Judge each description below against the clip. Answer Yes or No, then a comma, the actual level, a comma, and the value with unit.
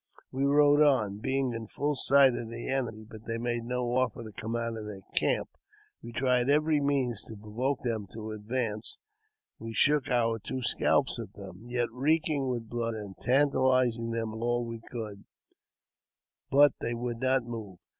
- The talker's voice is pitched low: Yes, low, 120 Hz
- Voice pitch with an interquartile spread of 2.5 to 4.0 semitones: Yes, average, 2.8 semitones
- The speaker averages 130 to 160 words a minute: No, average, 175 wpm